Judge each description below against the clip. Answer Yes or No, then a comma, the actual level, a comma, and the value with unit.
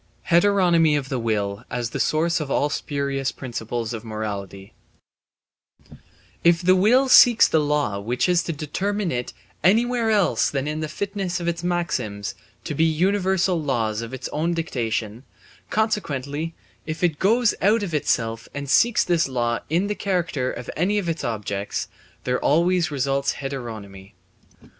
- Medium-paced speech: Yes, average, 155 wpm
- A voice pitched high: No, medium, 150 Hz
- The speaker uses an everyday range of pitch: No, wide, 7.0 semitones